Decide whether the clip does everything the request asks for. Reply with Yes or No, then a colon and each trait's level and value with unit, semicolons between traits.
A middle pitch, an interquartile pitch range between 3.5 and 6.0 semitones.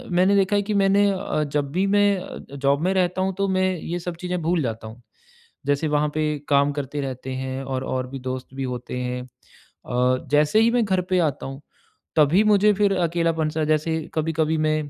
Yes: medium, 155 Hz; wide, 5.5 semitones